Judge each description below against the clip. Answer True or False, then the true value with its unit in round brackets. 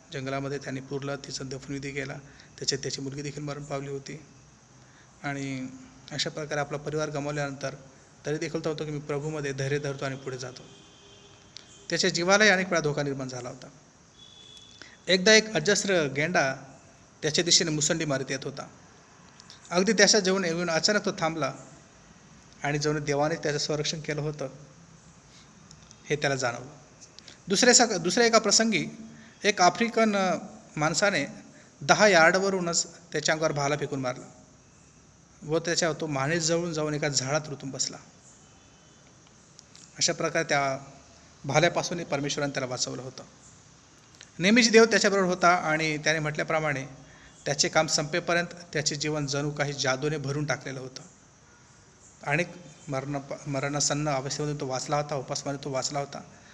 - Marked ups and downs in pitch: False (3.4 semitones)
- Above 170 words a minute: False (135 wpm)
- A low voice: False (150 Hz)